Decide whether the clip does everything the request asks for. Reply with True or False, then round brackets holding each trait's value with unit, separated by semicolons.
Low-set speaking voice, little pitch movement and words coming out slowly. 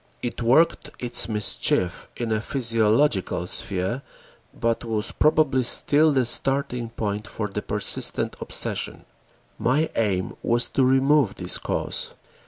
False (120 Hz; 4.2 semitones; 125 wpm)